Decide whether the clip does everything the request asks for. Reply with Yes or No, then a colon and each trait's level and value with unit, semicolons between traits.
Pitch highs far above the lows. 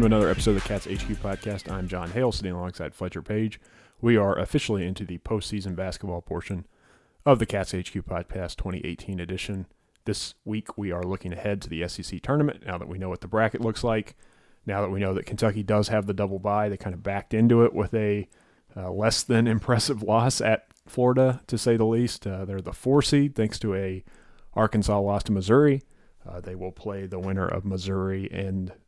No: average, 3.0 semitones